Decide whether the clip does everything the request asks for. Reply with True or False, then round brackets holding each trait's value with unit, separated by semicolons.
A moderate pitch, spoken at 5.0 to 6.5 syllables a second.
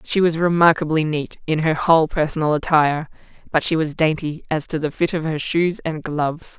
True (155 Hz; 5.4 syllables/s)